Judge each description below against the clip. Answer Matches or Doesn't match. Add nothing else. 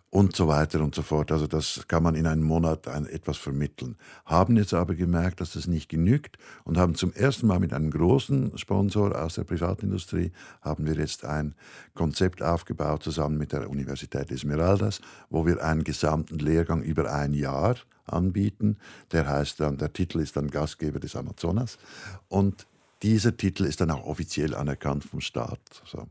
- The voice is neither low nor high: Doesn't match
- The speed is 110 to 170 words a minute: Doesn't match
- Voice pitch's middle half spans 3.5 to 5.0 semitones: Matches